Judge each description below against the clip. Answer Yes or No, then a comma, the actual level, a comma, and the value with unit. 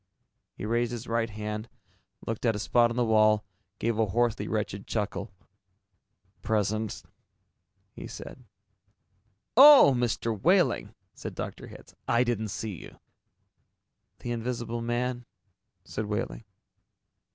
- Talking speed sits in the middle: No, slow, 120 wpm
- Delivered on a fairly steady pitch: Yes, narrow, 1.9 semitones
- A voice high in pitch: No, low, 115 Hz